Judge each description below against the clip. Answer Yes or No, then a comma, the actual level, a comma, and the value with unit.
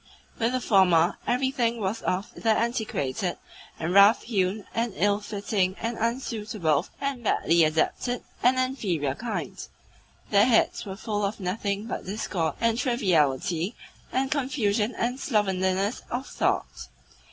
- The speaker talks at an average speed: No, slow, 130 wpm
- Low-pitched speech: No, high, 210 Hz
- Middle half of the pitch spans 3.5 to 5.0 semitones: Yes, average, 4.2 semitones